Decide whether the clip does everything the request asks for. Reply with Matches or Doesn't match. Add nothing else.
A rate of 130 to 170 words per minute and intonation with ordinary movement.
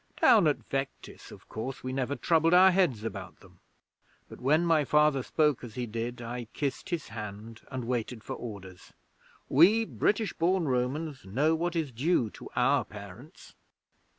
Doesn't match